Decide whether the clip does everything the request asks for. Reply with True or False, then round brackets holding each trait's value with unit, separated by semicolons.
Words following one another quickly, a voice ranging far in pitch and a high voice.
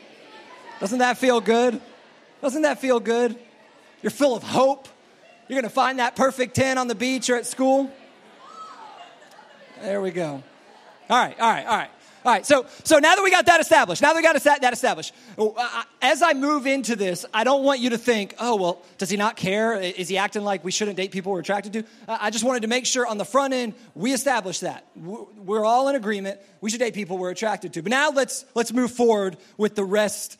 False (215 wpm; 4.3 semitones; 235 Hz)